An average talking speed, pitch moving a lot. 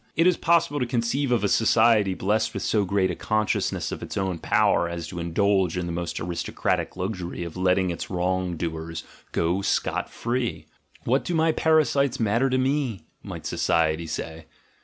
Yes: average, 185 wpm; wide, 5.8 semitones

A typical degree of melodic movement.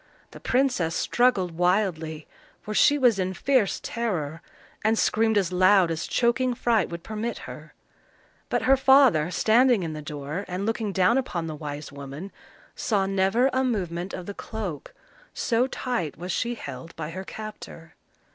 No: wide, 6.0 semitones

